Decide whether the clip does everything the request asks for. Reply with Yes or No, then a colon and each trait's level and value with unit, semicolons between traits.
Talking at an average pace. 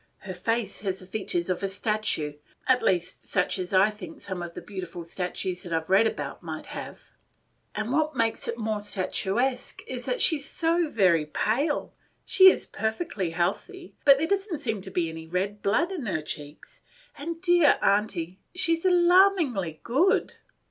Yes: average, 185 wpm